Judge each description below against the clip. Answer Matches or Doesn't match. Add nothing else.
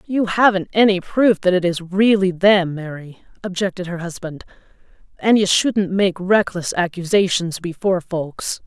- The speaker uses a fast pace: Doesn't match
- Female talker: Matches